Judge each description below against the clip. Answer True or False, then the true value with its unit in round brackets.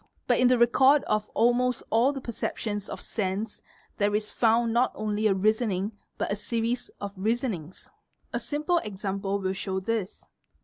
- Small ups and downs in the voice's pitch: False (3.1 semitones)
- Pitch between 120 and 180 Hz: False (215 Hz)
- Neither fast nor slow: True (170 wpm)